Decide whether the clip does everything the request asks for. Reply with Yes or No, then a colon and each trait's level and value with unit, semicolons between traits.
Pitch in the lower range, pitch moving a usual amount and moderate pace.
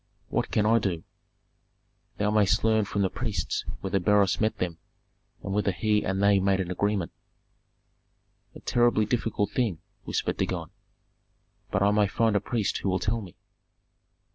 No: low, 105 Hz; narrow, 2.0 semitones; average, 160 wpm